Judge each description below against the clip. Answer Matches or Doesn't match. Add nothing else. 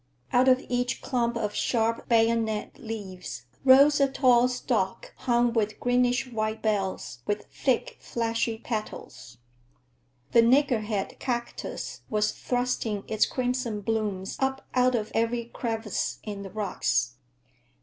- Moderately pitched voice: Doesn't match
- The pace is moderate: Doesn't match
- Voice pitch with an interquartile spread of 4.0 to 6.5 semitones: Doesn't match